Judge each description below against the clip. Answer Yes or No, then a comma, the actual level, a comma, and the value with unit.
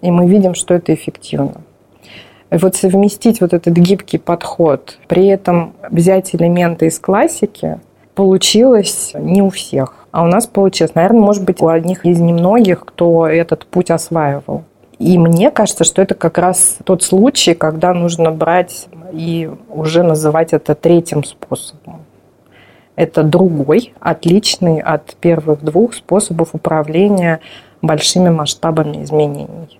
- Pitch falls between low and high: Yes, medium, 170 Hz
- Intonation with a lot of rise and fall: No, average, 2.7 semitones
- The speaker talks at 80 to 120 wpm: No, average, 135 wpm